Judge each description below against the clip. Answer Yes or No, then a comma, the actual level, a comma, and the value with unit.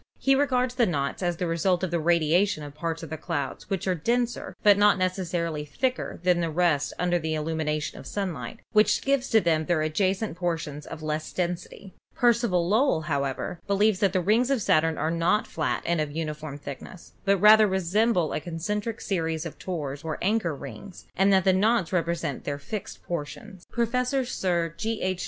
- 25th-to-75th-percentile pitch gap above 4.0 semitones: Yes, average, 4.6 semitones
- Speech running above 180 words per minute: Yes, average, 190 wpm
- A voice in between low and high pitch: Yes, medium, 175 Hz